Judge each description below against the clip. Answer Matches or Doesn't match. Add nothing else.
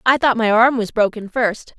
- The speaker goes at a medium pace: Doesn't match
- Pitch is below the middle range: Doesn't match